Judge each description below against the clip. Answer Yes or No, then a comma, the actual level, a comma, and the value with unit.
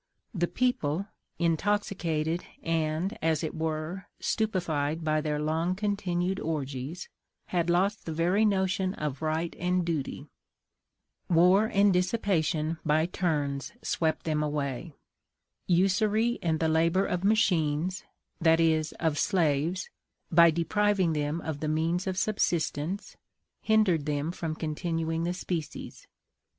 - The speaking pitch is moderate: Yes, medium, 165 Hz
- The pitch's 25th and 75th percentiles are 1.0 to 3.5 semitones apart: Yes, average, 3.2 semitones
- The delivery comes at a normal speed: No, slow, 120 wpm